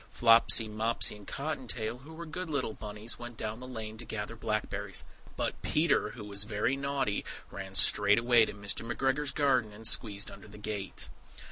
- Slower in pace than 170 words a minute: No, average, 180 wpm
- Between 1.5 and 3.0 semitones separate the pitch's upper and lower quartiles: No, average, 3.7 semitones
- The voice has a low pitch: Yes, low, 115 Hz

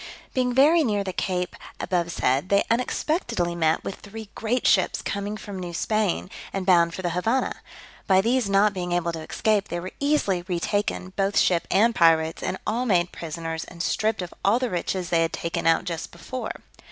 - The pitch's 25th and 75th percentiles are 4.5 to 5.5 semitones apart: No, average, 4.0 semitones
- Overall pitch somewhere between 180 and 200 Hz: Yes, high, 190 Hz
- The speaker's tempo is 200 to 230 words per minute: No, average, 190 wpm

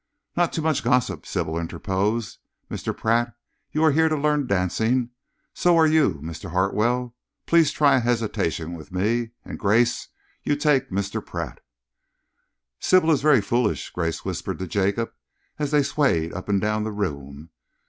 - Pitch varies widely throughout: Yes, wide, 7.4 semitones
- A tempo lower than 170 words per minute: Yes, average, 160 wpm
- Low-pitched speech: Yes, low, 115 Hz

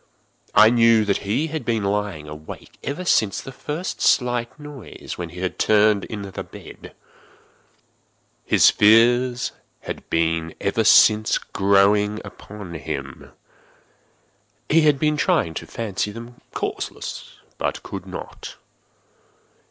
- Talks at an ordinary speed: No, slow, 125 wpm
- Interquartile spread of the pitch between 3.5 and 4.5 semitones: Yes, average, 3.8 semitones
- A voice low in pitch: Yes, low, 110 Hz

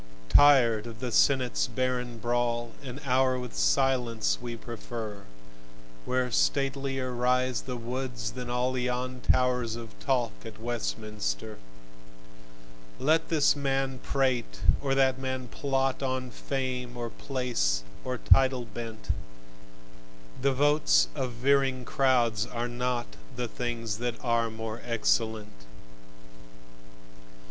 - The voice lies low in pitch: Yes, low, 125 Hz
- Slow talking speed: Yes, slow, 115 wpm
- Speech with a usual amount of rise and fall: No, narrow, 2.1 semitones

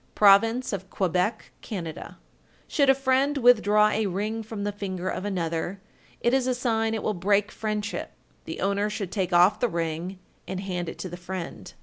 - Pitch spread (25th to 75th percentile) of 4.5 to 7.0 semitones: No, average, 3.3 semitones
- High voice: Yes, high, 205 Hz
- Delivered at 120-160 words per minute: No, average, 190 wpm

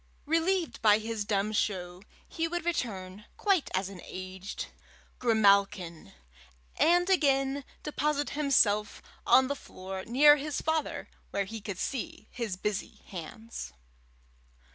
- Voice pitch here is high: Yes, high, 225 Hz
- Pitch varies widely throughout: Yes, wide, 7.0 semitones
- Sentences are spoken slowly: Yes, slow, 120 wpm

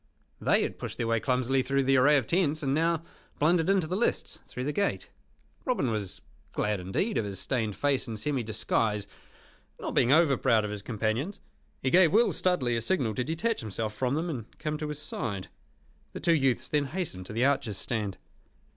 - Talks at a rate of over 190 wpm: Yes, average, 200 wpm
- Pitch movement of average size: No, wide, 6.1 semitones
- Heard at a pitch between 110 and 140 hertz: Yes, low, 135 Hz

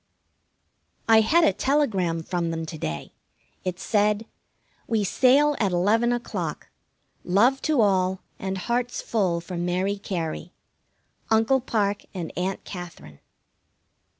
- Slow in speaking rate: Yes, slow, 125 wpm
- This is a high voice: Yes, high, 200 Hz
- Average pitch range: Yes, average, 4.7 semitones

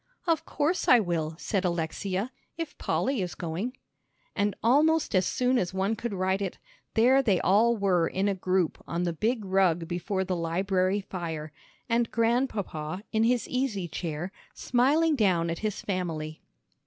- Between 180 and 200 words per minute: No, average, 160 wpm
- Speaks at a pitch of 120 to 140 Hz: No, high, 195 Hz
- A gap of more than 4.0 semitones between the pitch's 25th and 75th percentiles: Yes, average, 5.1 semitones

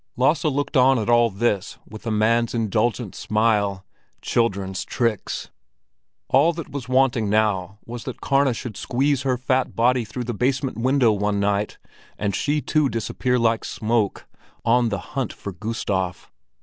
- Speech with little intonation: No, average, 3.6 semitones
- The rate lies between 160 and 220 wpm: No, average, 150 wpm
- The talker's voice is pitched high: No, low, 115 Hz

